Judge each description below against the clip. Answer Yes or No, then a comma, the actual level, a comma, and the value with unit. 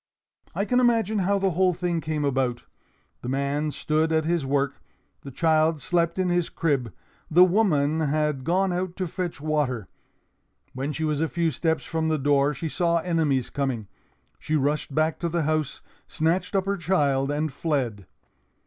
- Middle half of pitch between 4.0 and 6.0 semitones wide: No, average, 3.5 semitones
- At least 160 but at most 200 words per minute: Yes, average, 175 wpm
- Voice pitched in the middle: Yes, medium, 155 Hz